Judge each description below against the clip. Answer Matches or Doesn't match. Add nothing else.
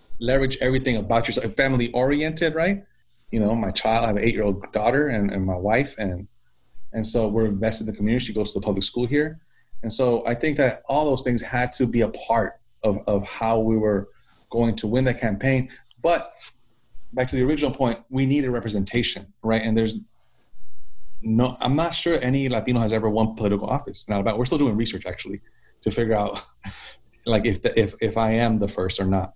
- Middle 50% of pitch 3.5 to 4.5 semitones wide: Doesn't match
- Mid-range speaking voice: Doesn't match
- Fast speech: Matches